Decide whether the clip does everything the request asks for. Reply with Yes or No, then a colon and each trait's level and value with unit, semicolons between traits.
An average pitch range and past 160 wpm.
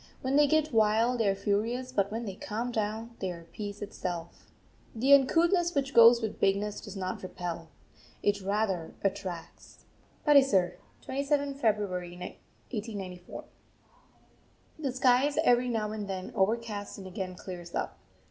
No: average, 4.6 semitones; average, 145 wpm